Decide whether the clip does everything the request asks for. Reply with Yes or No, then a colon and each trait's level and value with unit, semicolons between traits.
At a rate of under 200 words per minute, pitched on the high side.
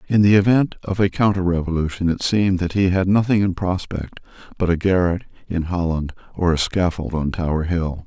No: average, 185 wpm; very low, 90 Hz